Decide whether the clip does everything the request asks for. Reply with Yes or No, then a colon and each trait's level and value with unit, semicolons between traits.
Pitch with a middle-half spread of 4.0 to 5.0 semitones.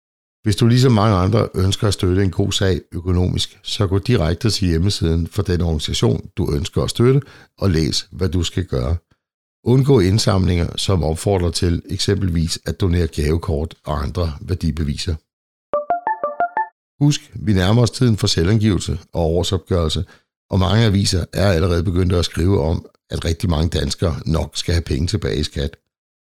Yes: average, 4.3 semitones